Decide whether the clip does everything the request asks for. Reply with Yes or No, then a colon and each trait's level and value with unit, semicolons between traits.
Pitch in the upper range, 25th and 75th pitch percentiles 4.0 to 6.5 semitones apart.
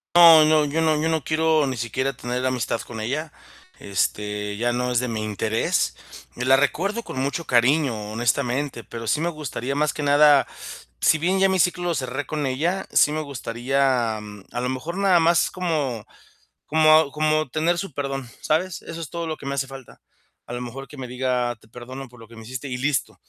No: low, 135 Hz; average, 4.3 semitones